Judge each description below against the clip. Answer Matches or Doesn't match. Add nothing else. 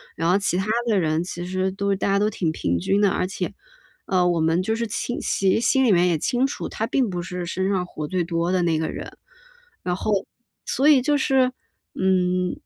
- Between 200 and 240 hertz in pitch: Doesn't match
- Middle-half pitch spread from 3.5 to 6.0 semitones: Doesn't match